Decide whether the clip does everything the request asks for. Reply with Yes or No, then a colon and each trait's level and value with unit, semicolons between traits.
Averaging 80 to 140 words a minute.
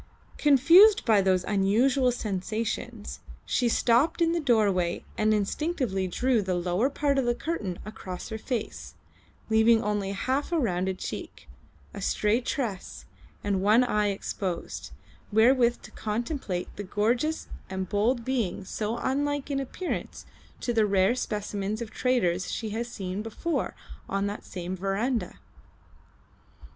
Yes: slow, 135 wpm